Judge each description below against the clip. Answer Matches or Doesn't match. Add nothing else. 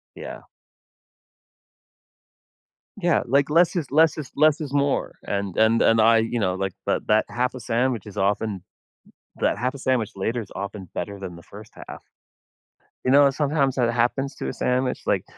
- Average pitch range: Matches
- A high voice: Doesn't match